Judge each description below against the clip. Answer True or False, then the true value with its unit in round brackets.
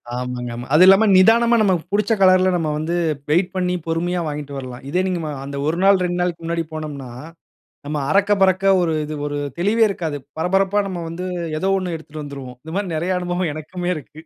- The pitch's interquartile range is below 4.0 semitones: True (3.6 semitones)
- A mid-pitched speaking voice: True (175 Hz)